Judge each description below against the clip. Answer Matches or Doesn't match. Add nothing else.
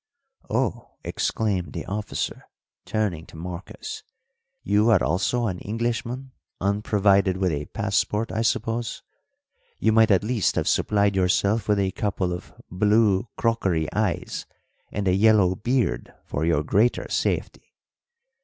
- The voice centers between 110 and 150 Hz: Doesn't match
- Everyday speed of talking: Doesn't match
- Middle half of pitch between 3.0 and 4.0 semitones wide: Matches